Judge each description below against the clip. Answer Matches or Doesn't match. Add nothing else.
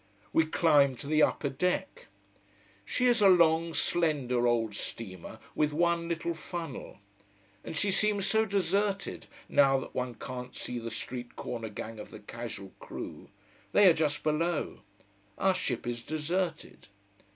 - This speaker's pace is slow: Doesn't match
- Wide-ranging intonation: Matches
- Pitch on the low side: Doesn't match